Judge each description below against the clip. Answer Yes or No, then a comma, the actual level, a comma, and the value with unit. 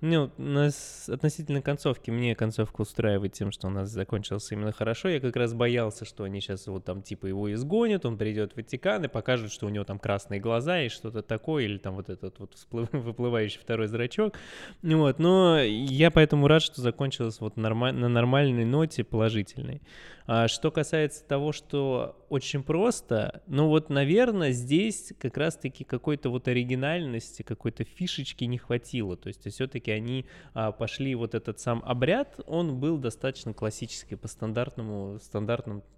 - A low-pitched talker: Yes, low, 120 Hz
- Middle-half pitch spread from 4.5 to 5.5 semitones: Yes, average, 4.9 semitones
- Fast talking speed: Yes, fast, 170 wpm